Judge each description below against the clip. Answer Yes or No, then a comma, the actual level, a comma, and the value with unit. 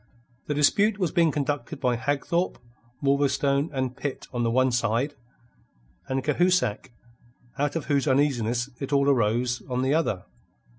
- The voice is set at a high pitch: No, medium, 140 Hz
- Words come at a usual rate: Yes, average, 145 wpm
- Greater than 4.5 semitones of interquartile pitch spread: No, average, 2.8 semitones